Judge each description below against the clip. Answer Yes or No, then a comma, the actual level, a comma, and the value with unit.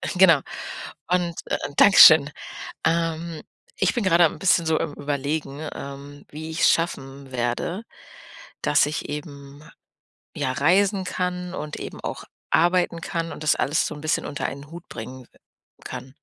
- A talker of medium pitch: Yes, medium, 155 Hz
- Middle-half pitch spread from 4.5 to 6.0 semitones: No, average, 3.4 semitones